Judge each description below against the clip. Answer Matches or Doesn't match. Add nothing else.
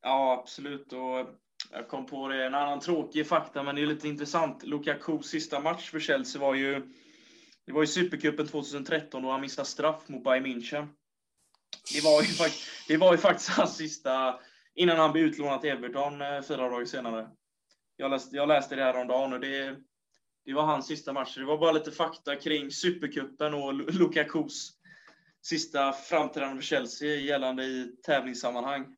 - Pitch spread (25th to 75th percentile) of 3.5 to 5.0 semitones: Doesn't match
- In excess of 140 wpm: Matches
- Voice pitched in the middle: Matches